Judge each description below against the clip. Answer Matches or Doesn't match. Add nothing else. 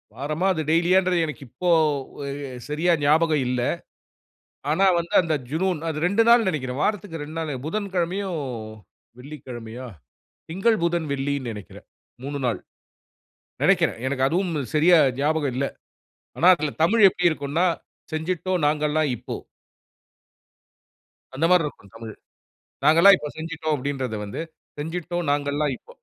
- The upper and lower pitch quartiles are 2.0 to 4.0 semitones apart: Matches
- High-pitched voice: Doesn't match